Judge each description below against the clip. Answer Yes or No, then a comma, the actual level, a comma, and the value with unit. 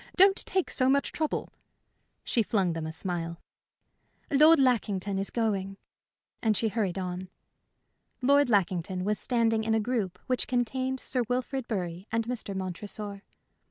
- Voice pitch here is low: No, high, 220 Hz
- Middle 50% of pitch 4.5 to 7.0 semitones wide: Yes, average, 5.1 semitones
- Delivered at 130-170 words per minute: Yes, average, 145 wpm